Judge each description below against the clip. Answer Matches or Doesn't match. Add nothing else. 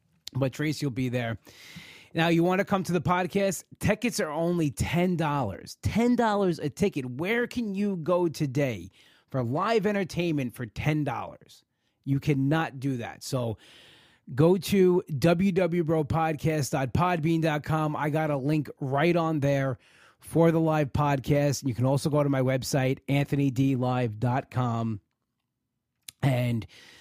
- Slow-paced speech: Matches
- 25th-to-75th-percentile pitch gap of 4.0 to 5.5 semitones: Matches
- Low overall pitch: Doesn't match